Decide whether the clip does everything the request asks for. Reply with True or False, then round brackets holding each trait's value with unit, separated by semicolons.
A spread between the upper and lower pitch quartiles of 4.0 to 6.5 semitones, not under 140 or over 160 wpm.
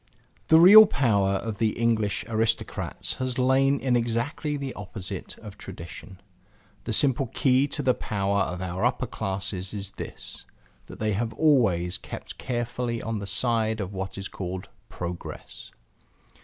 True (4.6 semitones; 150 wpm)